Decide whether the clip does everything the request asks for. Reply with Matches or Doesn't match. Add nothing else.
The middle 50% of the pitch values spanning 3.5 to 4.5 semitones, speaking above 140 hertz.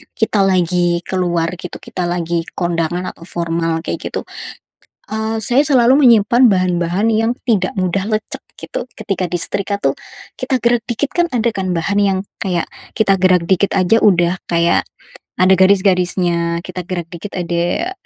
Matches